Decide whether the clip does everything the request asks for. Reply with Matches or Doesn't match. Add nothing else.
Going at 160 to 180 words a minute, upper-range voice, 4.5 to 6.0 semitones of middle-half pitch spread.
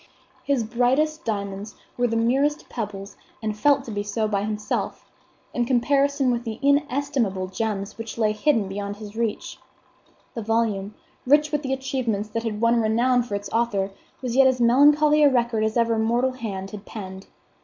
Doesn't match